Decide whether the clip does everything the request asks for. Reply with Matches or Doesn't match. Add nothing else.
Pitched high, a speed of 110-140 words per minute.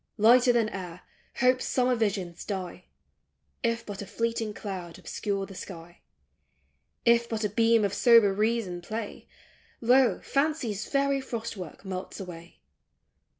Matches